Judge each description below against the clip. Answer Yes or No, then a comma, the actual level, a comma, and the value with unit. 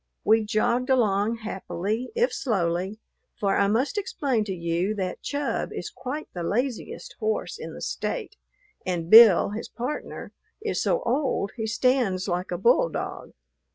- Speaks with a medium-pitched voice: No, high, 220 Hz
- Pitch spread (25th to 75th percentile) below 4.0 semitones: No, average, 5.1 semitones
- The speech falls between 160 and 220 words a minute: No, average, 150 wpm